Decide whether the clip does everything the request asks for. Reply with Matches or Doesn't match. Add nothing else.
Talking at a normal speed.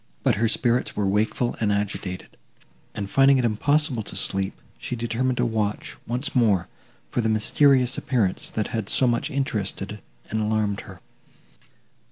Matches